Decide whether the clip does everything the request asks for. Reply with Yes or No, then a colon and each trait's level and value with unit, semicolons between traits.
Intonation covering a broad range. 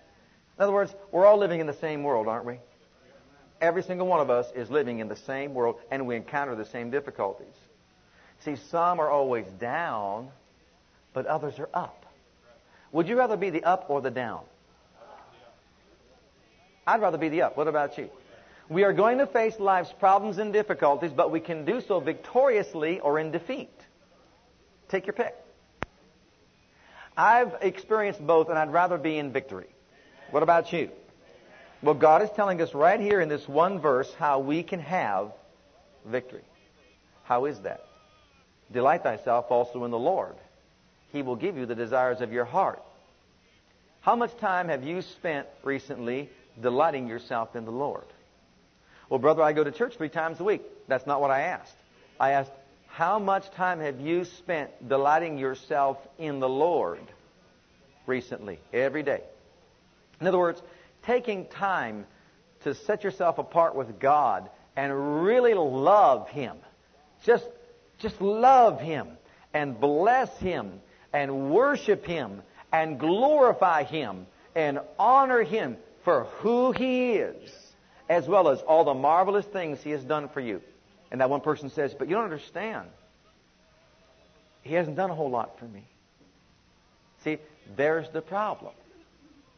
Yes: wide, 5.9 semitones